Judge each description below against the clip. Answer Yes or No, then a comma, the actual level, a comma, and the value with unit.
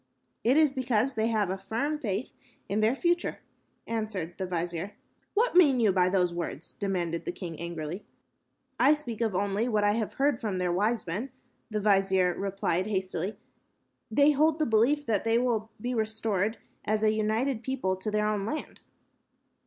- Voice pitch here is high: Yes, high, 215 Hz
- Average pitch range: Yes, average, 4.3 semitones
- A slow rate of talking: No, average, 175 wpm